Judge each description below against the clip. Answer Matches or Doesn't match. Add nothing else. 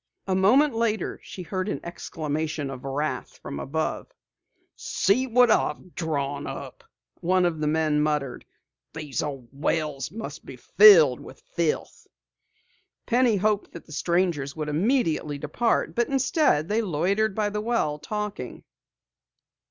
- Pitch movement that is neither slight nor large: Doesn't match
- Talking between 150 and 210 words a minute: Doesn't match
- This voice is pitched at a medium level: Matches